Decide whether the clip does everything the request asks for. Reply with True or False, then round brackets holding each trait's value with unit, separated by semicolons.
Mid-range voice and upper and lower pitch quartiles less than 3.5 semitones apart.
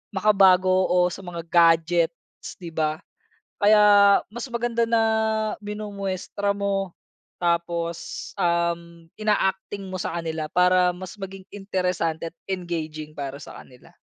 True (180 Hz; 2.9 semitones)